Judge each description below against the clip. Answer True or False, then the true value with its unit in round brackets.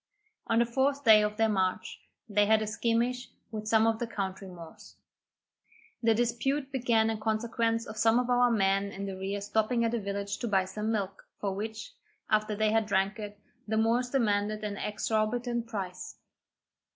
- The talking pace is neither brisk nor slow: True (180 wpm)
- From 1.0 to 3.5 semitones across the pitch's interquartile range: True (2.4 semitones)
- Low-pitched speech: False (220 Hz)